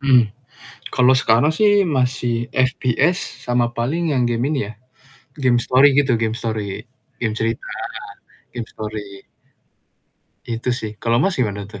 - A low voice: Yes, low, 120 Hz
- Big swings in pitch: No, average, 2.8 semitones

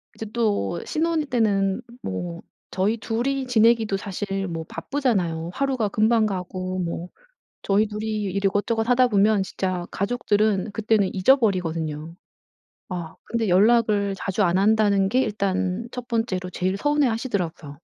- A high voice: Yes, high, 205 Hz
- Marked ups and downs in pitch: No, average, 3.6 semitones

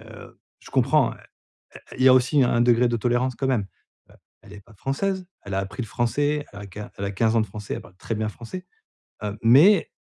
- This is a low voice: Yes, low, 120 Hz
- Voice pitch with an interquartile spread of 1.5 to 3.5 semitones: No, average, 4.0 semitones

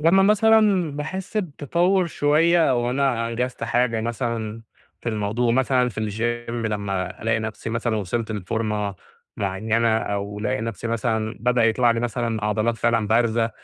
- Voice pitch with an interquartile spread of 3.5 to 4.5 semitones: No, average, 2.7 semitones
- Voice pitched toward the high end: No, low, 115 Hz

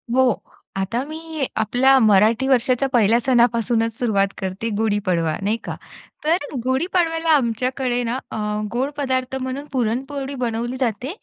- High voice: Yes, high, 245 Hz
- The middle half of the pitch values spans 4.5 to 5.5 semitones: No, average, 3.2 semitones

